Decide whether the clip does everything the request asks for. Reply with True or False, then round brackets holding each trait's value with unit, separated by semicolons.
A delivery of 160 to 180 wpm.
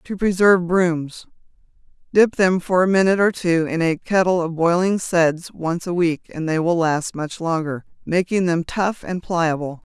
True (175 wpm)